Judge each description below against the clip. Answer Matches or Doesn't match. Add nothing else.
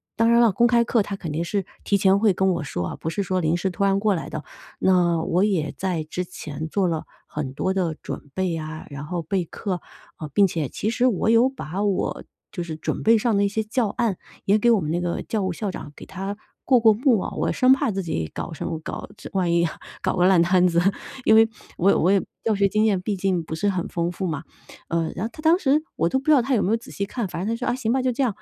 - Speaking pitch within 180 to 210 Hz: Matches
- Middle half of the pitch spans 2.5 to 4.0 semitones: Doesn't match